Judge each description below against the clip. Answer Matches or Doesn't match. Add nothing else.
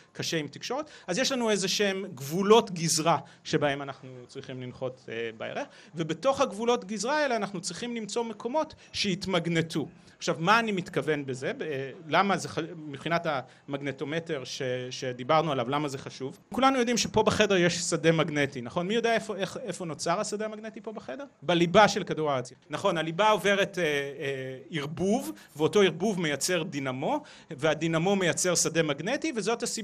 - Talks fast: Matches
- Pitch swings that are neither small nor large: Doesn't match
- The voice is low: Doesn't match